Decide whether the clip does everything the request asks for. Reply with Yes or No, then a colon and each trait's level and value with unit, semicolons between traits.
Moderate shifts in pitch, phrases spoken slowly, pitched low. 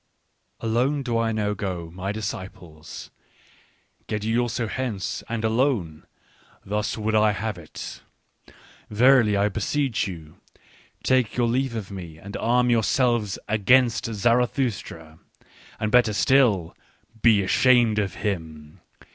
Yes: average, 3.8 semitones; slow, 130 wpm; low, 110 Hz